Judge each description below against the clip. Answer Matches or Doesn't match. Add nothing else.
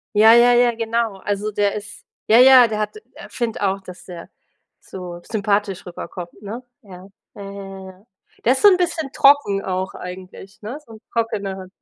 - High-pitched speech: Matches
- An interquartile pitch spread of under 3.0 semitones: Doesn't match